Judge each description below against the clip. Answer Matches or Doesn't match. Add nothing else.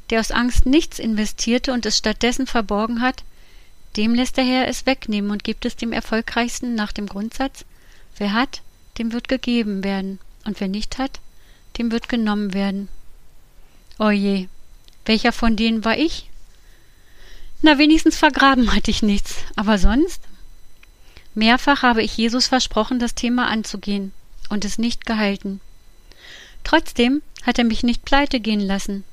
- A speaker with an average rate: Matches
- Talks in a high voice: Matches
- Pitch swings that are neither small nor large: Matches